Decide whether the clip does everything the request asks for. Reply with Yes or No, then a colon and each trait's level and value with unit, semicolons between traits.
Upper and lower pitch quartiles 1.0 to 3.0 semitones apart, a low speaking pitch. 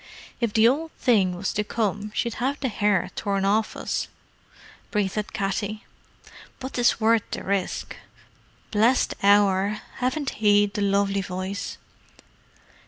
No: narrow, 2.6 semitones; high, 210 Hz